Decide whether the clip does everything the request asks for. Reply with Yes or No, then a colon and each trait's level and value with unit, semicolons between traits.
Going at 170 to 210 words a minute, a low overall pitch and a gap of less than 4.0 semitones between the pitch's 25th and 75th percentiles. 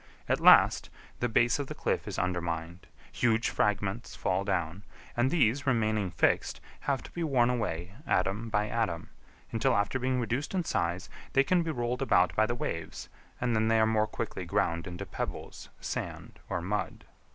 No: average, 175 wpm; low, 110 Hz; average, 5.0 semitones